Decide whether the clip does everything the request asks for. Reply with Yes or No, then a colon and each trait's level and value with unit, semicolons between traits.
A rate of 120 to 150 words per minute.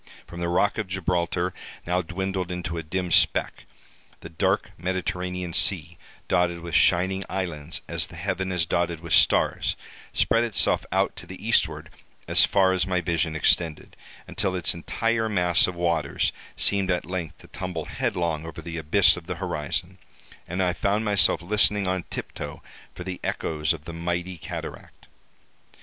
No: average, 165 wpm